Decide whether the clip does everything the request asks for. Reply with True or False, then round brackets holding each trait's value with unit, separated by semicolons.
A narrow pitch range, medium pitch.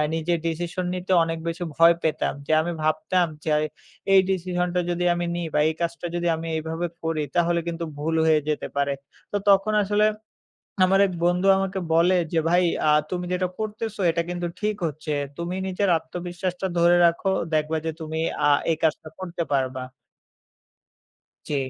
True (2.0 semitones; 175 Hz)